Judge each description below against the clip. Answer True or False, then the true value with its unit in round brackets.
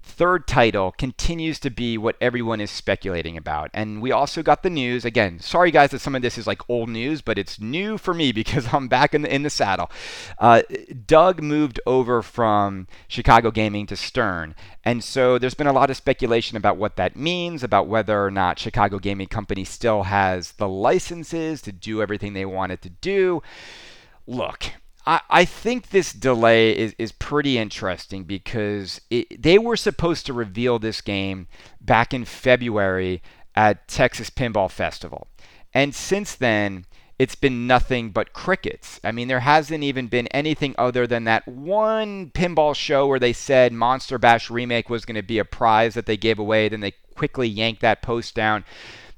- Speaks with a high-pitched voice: False (120 Hz)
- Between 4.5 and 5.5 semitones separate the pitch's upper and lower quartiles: True (5.2 semitones)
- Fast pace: False (180 wpm)